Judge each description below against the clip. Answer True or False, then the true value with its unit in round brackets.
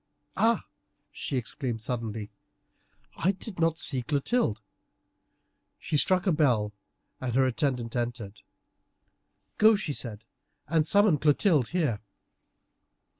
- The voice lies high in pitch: False (140 Hz)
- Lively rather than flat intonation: True (6.3 semitones)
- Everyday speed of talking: False (110 wpm)